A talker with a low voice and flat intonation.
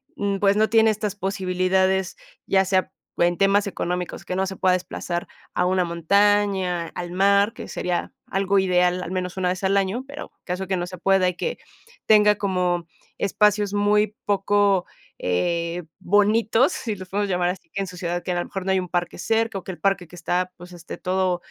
No: high, 190 Hz; narrow, 2.1 semitones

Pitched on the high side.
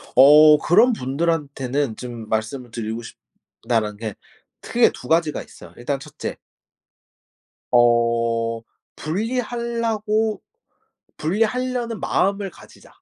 No: medium, 145 Hz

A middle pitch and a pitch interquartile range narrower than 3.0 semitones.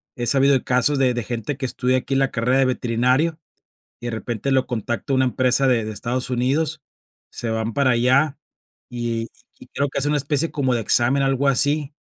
No: low, 130 Hz; narrow, 2.5 semitones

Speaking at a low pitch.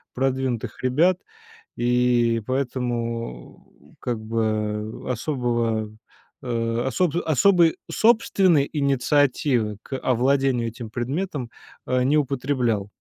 Yes: low, 125 Hz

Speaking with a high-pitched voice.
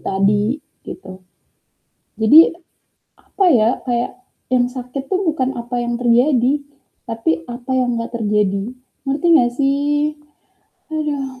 Yes: high, 245 Hz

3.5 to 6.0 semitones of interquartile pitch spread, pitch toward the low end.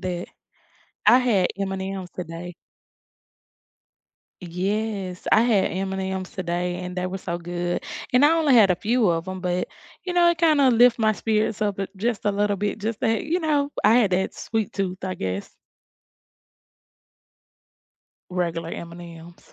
No: average, 3.8 semitones; high, 190 Hz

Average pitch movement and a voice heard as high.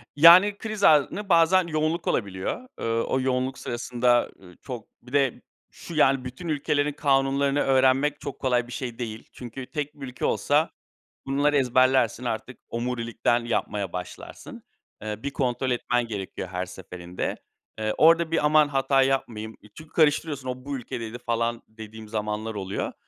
No: average, 4.1 semitones; low, 130 Hz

